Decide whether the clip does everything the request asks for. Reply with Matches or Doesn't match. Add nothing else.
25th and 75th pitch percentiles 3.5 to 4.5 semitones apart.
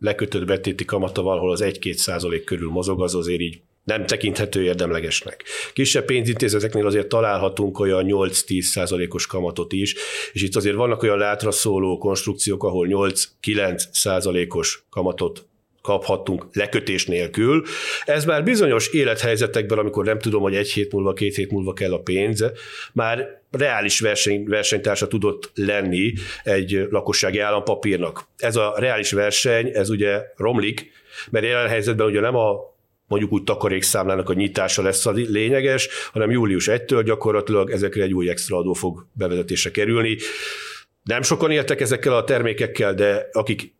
Doesn't match